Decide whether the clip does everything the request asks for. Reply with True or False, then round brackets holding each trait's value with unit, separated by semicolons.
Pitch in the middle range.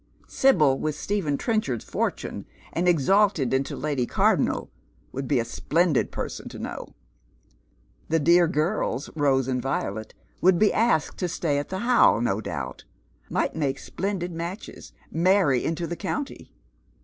True (160 Hz)